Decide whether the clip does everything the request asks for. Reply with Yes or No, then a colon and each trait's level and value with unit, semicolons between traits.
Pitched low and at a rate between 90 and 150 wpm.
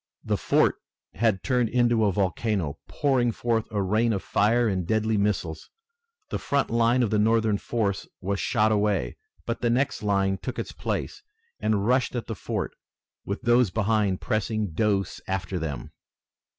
No: low, 110 Hz; average, 165 wpm